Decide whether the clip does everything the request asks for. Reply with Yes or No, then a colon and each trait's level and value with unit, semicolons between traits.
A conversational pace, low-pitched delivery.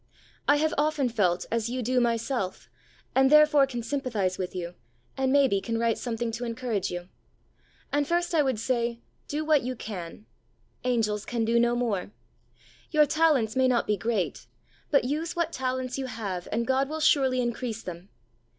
No: average, 180 wpm; high, 245 Hz